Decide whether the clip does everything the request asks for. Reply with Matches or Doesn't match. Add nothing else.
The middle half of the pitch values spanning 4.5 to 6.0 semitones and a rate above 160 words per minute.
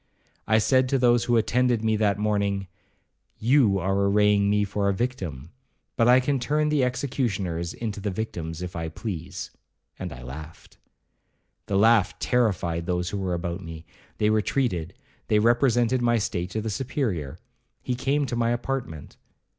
Doesn't match